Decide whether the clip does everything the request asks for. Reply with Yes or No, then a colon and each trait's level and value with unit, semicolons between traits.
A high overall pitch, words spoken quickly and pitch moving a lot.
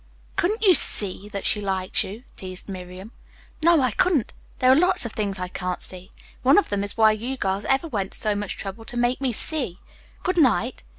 Yes: high, 215 Hz; fast, 215 wpm; wide, 5.7 semitones